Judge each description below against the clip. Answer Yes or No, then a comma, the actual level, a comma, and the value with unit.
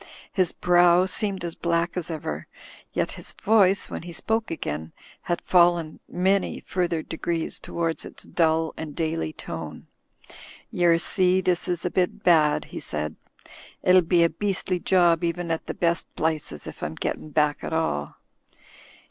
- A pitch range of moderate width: No, narrow, 2.0 semitones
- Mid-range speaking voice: Yes, medium, 170 Hz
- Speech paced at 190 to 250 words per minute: No, average, 155 wpm